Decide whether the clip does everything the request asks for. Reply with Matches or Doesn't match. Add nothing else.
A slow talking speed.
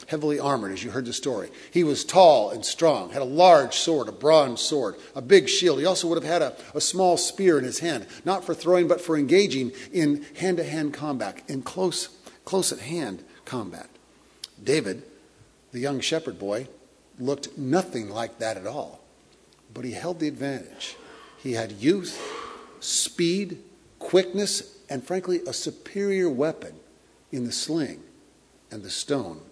Doesn't match